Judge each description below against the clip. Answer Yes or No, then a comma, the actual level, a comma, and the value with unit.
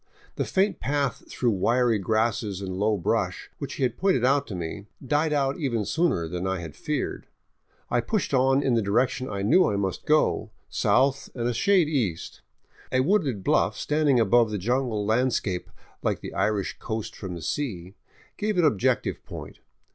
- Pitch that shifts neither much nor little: No, wide, 5.9 semitones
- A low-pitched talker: Yes, low, 120 Hz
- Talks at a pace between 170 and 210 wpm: Yes, average, 180 wpm